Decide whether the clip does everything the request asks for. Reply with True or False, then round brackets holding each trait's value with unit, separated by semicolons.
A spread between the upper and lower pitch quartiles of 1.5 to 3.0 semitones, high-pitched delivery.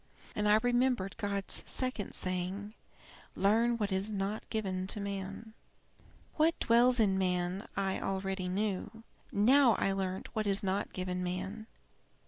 True (2.6 semitones; 200 Hz)